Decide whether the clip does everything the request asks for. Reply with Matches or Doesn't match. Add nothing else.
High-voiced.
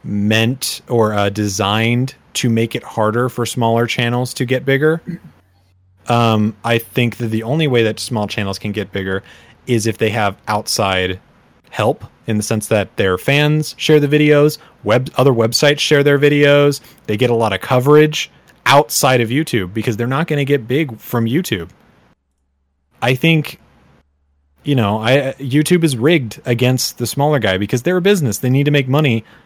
Doesn't match